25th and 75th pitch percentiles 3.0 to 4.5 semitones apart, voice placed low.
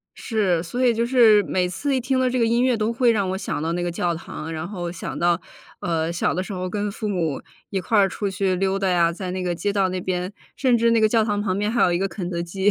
No: average, 3.9 semitones; high, 190 Hz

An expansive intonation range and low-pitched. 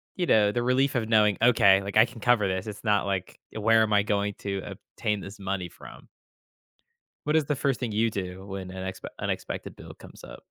No: average, 2.9 semitones; low, 105 Hz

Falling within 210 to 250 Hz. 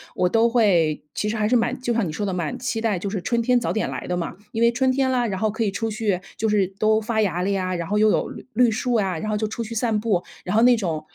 Yes: high, 215 Hz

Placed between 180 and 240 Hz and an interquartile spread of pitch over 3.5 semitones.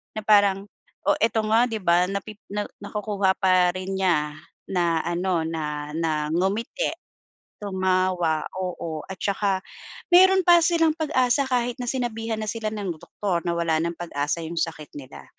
Yes: high, 190 Hz; average, 4.5 semitones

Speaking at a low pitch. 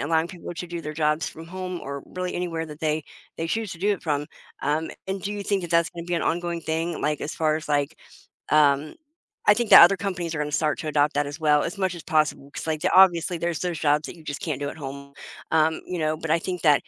No: medium, 160 Hz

